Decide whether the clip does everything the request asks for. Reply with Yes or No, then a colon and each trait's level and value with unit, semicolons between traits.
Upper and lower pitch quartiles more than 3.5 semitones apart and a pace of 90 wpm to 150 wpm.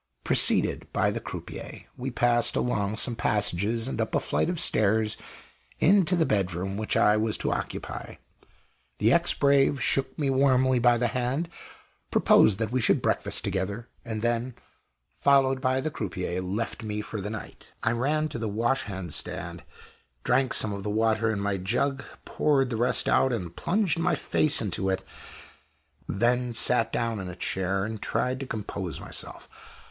No: average, 4.2 semitones; average, 170 wpm